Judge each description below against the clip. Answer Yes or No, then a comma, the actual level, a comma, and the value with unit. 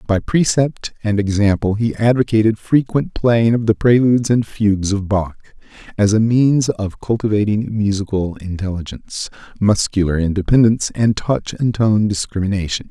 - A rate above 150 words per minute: No, slow, 135 wpm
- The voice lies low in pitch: Yes, low, 105 Hz